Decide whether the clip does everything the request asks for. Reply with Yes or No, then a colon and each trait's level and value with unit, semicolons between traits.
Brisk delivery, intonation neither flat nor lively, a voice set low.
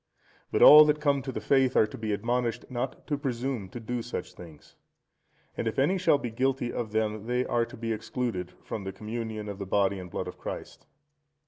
Yes: fast, 215 wpm; average, 3.6 semitones; low, 115 Hz